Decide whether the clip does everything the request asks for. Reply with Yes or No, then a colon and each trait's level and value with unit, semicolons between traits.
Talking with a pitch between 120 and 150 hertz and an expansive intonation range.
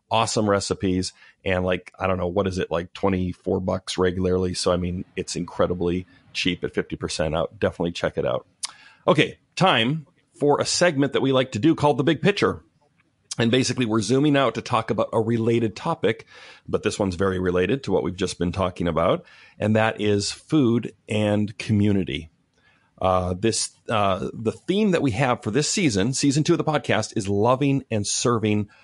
No: low, 105 Hz; wide, 5.7 semitones